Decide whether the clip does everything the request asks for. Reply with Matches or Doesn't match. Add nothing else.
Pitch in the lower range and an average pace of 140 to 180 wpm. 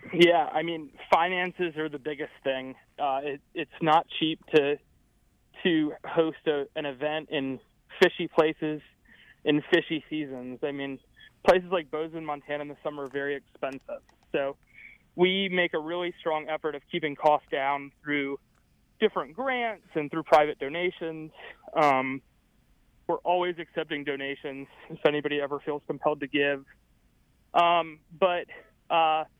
Doesn't match